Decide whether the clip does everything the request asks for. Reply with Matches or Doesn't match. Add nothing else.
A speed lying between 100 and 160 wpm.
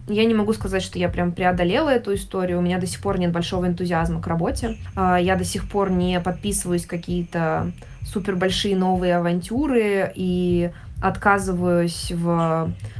Matches